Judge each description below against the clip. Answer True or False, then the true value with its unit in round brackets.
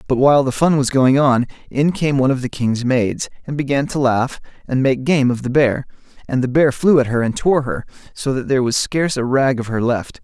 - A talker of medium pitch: False (130 Hz)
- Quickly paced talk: True (250 wpm)